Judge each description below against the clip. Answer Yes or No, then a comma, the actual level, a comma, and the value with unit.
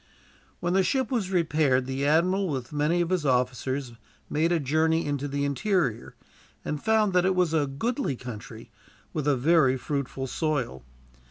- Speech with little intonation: No, average, 4.9 semitones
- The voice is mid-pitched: Yes, medium, 150 Hz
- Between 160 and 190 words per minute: Yes, average, 165 wpm